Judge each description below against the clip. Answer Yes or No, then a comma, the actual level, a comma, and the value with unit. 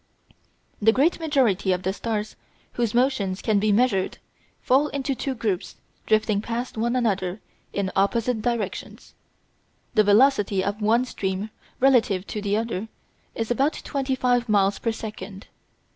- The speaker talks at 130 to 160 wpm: Yes, average, 145 wpm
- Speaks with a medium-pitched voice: No, high, 220 Hz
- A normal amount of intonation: Yes, average, 3.7 semitones